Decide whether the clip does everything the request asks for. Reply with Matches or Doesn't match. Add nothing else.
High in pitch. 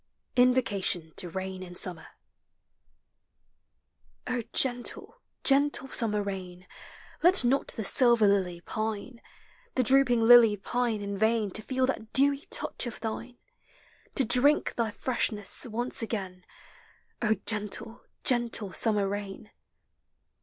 Matches